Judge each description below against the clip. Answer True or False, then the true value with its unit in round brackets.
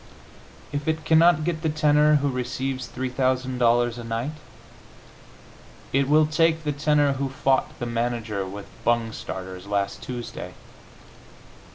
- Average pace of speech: False (130 wpm)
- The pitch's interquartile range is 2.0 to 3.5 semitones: False (4.2 semitones)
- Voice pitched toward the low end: True (130 Hz)